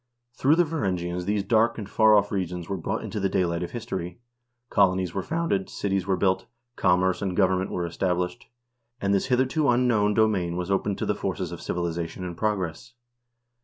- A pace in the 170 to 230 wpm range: Yes, average, 180 wpm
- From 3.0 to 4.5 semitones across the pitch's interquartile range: Yes, average, 3.4 semitones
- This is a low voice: Yes, very low, 95 Hz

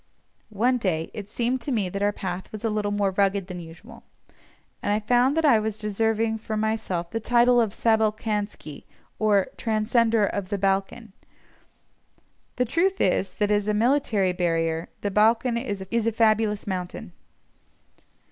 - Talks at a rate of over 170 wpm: No, average, 155 wpm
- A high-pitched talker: Yes, high, 215 Hz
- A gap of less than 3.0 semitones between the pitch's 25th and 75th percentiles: Yes, narrow, 2.6 semitones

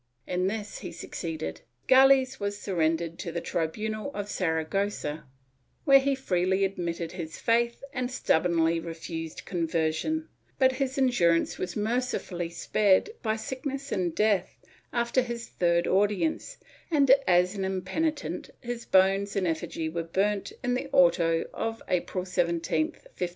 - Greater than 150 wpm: No, average, 140 wpm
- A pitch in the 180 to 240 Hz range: Yes, high, 190 Hz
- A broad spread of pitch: Yes, wide, 5.8 semitones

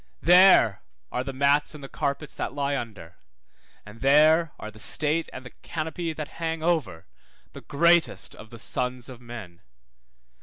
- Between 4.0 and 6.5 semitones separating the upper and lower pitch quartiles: Yes, average, 5.1 semitones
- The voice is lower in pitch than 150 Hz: Yes, medium, 140 Hz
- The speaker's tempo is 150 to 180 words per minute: Yes, average, 160 wpm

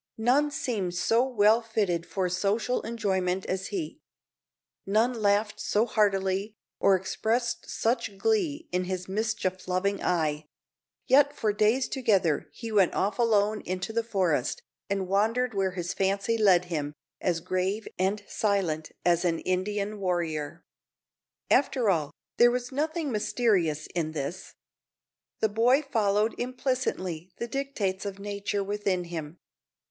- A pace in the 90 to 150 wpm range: Yes, slow, 135 wpm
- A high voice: Yes, high, 200 Hz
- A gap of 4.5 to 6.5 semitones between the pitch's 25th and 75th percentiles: No, average, 3.9 semitones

